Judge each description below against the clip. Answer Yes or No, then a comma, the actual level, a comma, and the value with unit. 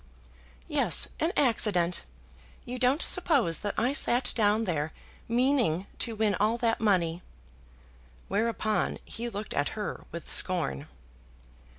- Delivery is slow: Yes, slow, 120 wpm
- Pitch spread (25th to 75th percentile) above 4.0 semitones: Yes, average, 4.8 semitones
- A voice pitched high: Yes, high, 215 Hz